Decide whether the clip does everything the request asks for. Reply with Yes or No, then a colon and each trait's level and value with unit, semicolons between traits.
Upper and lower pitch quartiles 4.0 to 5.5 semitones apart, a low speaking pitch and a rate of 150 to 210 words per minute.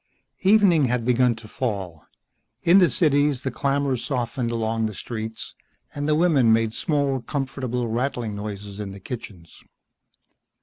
No: average, 4.3 semitones; low, 125 Hz; average, 140 wpm